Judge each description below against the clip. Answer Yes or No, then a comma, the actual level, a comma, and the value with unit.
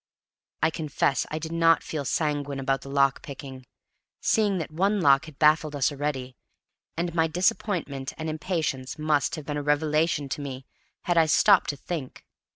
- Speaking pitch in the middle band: Yes, medium, 150 Hz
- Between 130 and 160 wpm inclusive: No, average, 170 wpm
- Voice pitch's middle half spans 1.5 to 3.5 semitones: Yes, average, 2.8 semitones